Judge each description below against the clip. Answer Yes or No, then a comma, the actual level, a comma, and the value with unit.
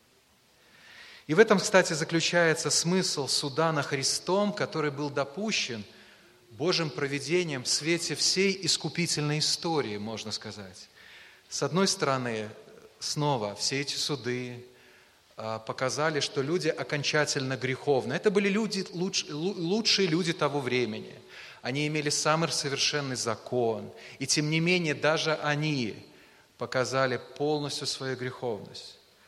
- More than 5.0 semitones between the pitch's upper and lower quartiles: No, average, 4.3 semitones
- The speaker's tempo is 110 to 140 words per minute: Yes, average, 115 wpm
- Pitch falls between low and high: Yes, medium, 150 Hz